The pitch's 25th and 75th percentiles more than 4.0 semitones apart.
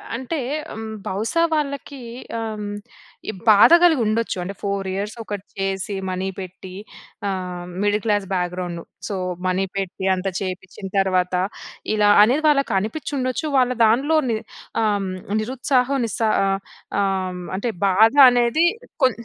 Yes: average, 4.7 semitones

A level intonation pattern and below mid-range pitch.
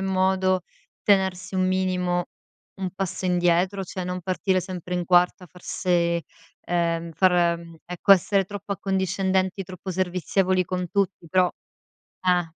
No: narrow, 1.2 semitones; medium, 185 Hz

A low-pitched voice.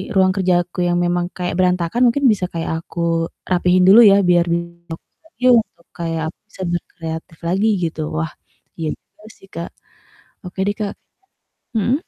No: medium, 175 Hz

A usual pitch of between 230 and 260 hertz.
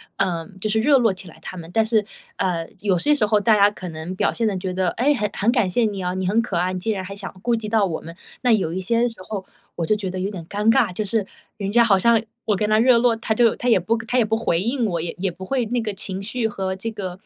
No: high, 205 Hz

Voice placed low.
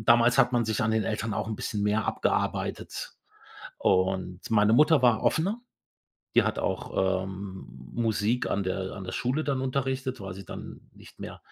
Yes: low, 110 Hz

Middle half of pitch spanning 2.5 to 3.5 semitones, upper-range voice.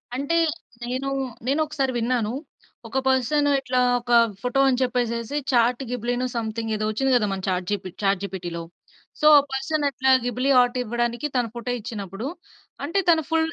Yes: average, 2.9 semitones; high, 245 Hz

